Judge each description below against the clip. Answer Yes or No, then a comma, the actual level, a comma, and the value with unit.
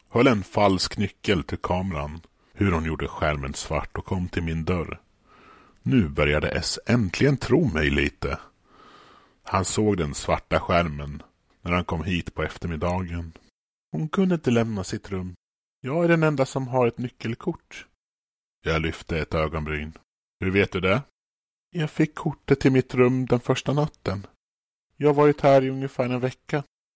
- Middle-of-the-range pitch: No, very low, 95 Hz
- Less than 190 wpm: Yes, average, 160 wpm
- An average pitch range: No, wide, 7.8 semitones